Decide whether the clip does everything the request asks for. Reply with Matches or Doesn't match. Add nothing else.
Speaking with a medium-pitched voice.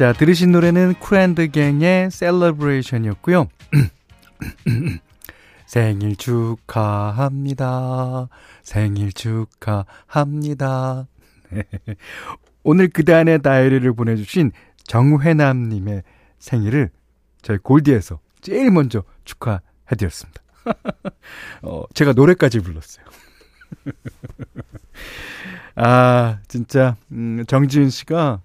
Doesn't match